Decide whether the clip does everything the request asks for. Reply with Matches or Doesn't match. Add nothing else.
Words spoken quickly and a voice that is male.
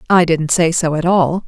Doesn't match